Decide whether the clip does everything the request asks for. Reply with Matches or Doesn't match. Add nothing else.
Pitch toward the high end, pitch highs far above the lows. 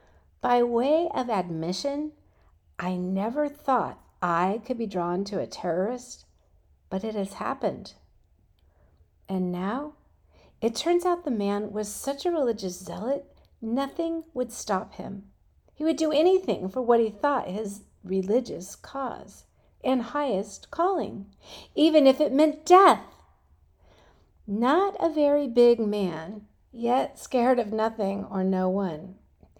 Matches